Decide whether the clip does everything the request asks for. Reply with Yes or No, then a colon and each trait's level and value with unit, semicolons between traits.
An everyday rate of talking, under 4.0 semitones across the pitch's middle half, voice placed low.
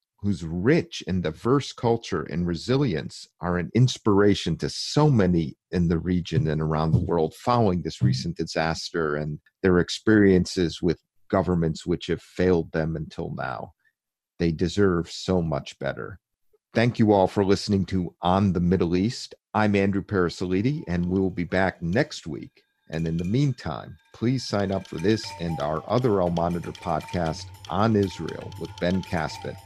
Yes: average, 160 wpm; average, 3.3 semitones; very low, 90 Hz